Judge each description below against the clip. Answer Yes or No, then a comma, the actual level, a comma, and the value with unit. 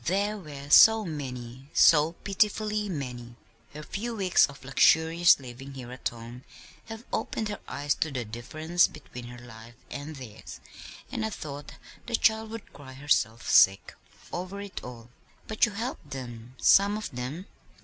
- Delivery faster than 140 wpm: Yes, average, 160 wpm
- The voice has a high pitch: No, medium, 145 Hz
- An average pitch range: No, wide, 8.2 semitones